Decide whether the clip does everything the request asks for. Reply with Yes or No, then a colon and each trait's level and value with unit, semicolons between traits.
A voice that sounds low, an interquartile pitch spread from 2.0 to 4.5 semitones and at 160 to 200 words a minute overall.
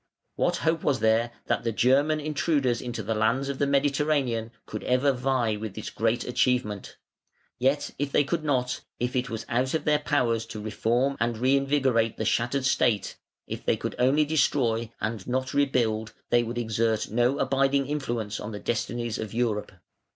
Yes: low, 125 Hz; average, 3.4 semitones; average, 175 wpm